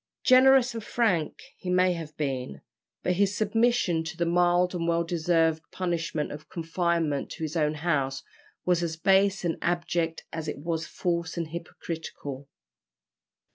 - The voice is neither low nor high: Yes, medium, 170 Hz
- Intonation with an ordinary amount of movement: No, narrow, 2.2 semitones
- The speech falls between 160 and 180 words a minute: No, average, 150 wpm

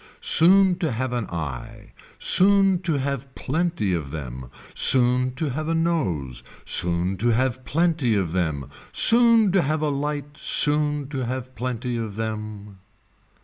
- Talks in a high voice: No, low, 130 Hz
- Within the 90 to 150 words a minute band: Yes, average, 145 wpm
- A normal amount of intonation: No, wide, 7.1 semitones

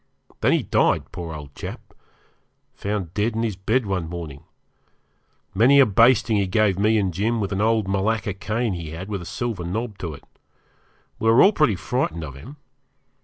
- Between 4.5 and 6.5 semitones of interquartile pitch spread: No, average, 4.1 semitones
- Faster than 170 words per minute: Yes, average, 185 wpm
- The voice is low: Yes, low, 100 Hz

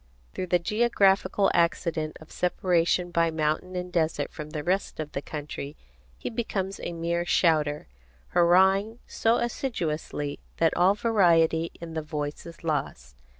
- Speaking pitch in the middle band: Yes, medium, 170 Hz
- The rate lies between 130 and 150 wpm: Yes, average, 145 wpm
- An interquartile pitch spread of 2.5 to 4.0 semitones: Yes, average, 3.4 semitones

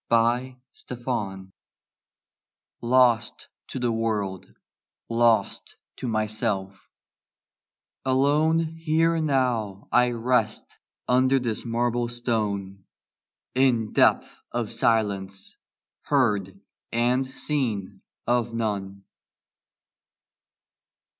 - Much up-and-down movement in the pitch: No, average, 3.3 semitones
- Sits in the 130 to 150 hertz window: No, low, 115 Hz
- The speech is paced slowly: Yes, slow, 75 wpm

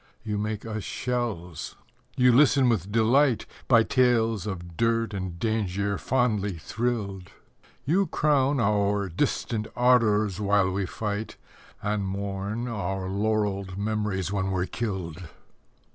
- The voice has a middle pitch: No, low, 105 Hz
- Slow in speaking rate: Yes, slow, 120 wpm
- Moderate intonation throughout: Yes, average, 3.2 semitones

